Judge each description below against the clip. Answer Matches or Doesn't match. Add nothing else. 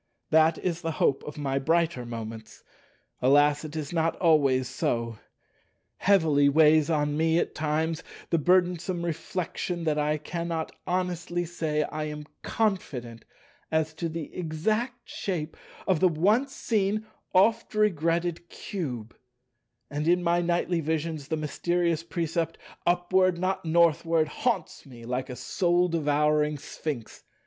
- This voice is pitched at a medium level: Matches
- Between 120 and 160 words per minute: Matches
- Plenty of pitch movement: Doesn't match